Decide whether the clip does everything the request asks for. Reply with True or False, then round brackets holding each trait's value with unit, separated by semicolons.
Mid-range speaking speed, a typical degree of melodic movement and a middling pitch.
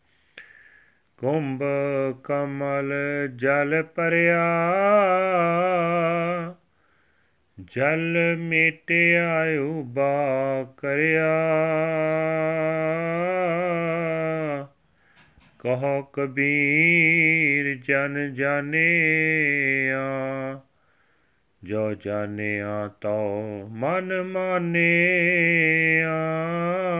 False (40 wpm; 3.5 semitones; 160 Hz)